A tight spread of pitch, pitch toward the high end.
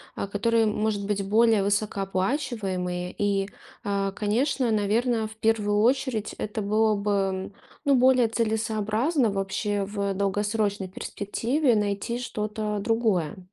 Yes: narrow, 2.2 semitones; high, 210 Hz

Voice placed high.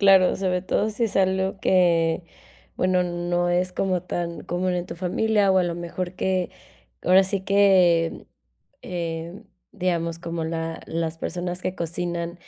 No: medium, 180 Hz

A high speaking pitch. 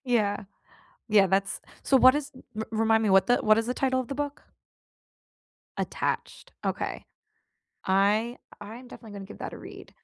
Yes: high, 225 Hz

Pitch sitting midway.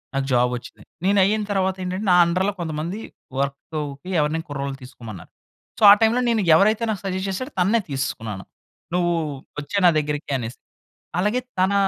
Yes: medium, 180 Hz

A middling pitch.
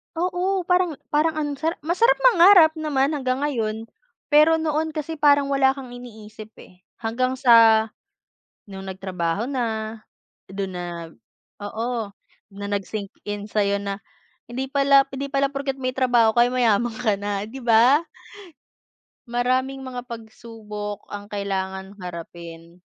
No: high, 240 Hz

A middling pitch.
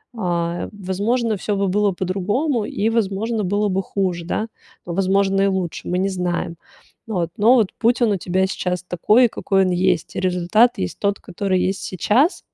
No: high, 195 Hz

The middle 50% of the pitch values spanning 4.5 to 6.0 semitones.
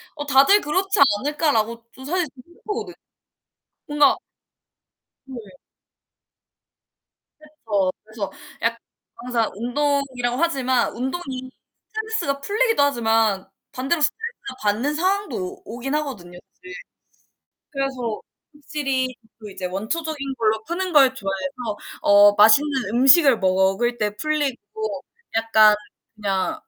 Yes: wide, 5.4 semitones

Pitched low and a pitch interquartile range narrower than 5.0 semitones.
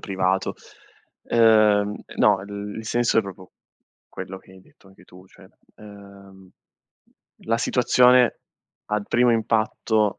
Yes: low, 105 Hz; average, 2.7 semitones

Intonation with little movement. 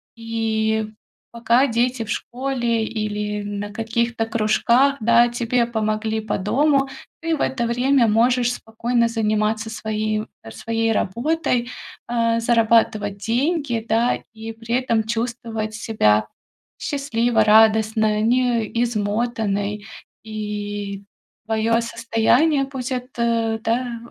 Yes: narrow, 1.8 semitones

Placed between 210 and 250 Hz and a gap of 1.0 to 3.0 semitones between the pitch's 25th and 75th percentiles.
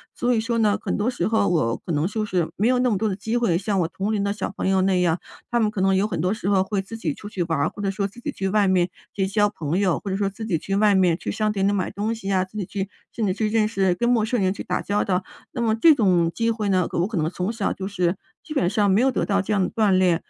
No: high, 200 Hz; narrow, 2.6 semitones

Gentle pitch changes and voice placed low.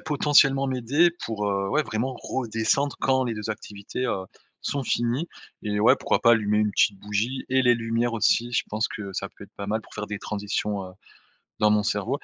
No: average, 3.8 semitones; low, 115 Hz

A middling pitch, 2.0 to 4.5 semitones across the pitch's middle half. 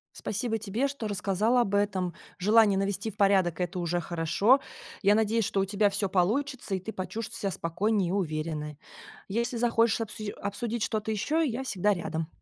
No: high, 205 Hz; average, 3.4 semitones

